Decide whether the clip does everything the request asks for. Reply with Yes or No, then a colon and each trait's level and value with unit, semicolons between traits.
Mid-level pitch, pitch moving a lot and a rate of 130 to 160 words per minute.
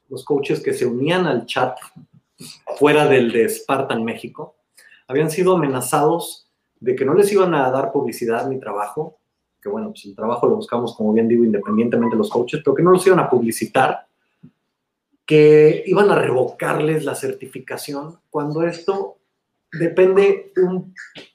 Yes: medium, 155 Hz; wide, 6.3 semitones; average, 155 wpm